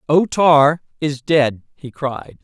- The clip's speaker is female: No, male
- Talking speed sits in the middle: Yes, average, 150 wpm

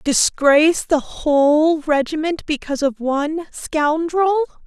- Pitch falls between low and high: No, very high, 305 Hz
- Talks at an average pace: No, slow, 105 wpm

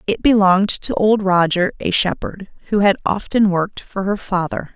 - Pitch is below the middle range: No, high, 195 Hz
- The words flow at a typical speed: Yes, average, 175 wpm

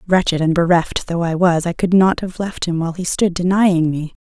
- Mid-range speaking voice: Yes, medium, 175 Hz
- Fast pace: Yes, fast, 240 wpm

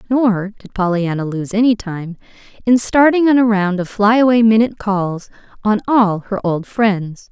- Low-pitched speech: No, high, 210 Hz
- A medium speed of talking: Yes, average, 170 wpm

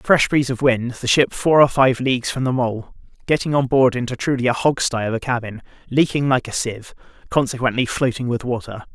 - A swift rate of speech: Yes, fast, 215 wpm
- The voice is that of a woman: No, male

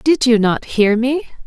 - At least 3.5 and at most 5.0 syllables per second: Yes, 3.8 syllables/s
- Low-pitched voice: No, high, 240 Hz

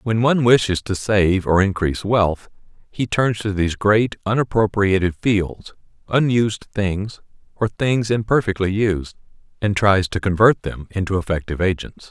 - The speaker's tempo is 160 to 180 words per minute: No, average, 145 wpm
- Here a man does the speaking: Yes, male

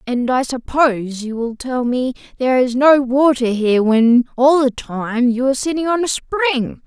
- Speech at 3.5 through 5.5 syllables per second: Yes, 4.6 syllables/s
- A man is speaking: Yes, male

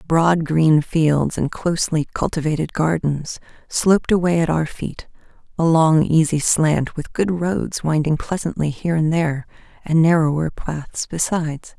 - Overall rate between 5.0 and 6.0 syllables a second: No, 4.5 syllables/s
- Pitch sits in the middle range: Yes, medium, 160 Hz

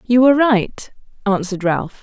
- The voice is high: Yes, high, 215 Hz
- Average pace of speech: Yes, average, 150 wpm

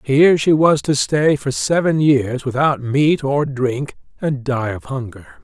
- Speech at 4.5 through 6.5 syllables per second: No, 4.1 syllables/s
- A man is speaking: Yes, male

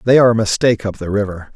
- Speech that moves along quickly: Yes, fast, 270 wpm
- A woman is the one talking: No, male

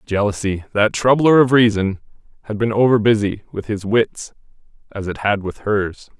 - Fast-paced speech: No, average, 165 wpm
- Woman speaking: No, male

